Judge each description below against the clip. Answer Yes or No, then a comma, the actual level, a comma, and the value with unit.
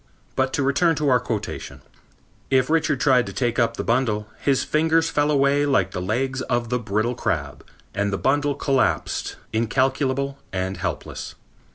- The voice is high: No, low, 130 Hz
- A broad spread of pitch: No, average, 3.7 semitones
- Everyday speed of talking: Yes, average, 165 wpm